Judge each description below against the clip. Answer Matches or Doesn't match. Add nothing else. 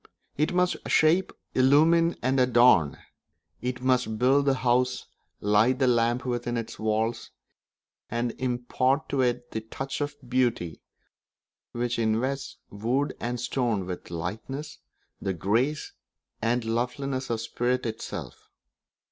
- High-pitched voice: Doesn't match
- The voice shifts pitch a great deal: Doesn't match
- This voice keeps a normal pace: Doesn't match